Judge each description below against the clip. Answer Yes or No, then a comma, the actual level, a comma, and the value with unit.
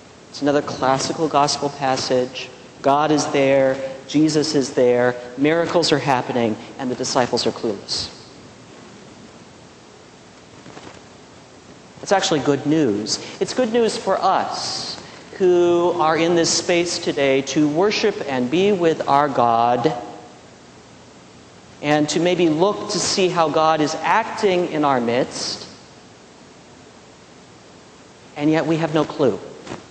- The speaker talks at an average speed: No, slow, 120 wpm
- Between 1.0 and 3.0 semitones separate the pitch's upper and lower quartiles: No, average, 4.4 semitones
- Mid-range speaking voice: Yes, medium, 150 Hz